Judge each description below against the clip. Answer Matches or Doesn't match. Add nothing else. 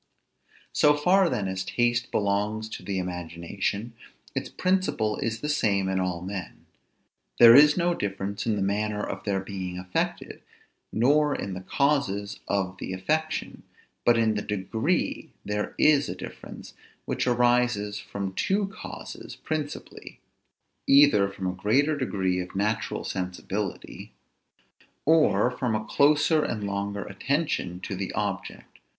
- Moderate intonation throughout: Doesn't match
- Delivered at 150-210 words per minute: Doesn't match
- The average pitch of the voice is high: Doesn't match